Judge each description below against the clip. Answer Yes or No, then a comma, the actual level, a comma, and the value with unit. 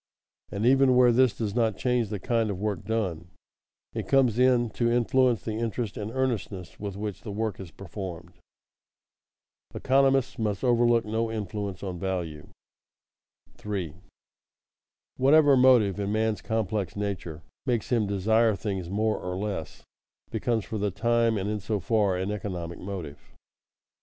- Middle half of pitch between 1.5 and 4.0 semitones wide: Yes, average, 3.4 semitones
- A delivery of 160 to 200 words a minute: No, average, 150 wpm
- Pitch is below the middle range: Yes, low, 105 Hz